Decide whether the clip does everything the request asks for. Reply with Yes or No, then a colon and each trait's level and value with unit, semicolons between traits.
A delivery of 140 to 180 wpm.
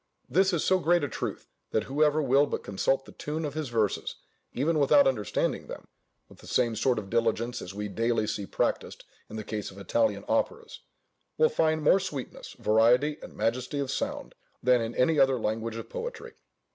No: average, 190 wpm